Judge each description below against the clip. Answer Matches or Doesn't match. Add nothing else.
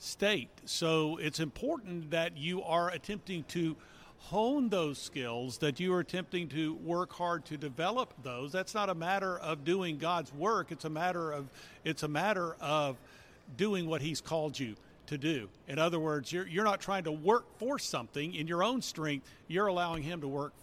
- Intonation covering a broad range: Doesn't match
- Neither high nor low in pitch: Matches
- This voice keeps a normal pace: Matches